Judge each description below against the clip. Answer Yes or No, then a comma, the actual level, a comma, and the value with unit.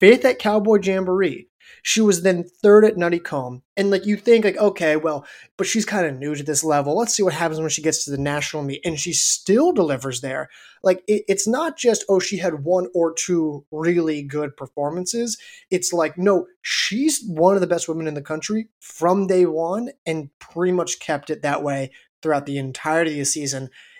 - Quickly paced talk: Yes, fast, 210 wpm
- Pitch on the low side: No, medium, 175 Hz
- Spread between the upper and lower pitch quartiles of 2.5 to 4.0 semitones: No, average, 4.7 semitones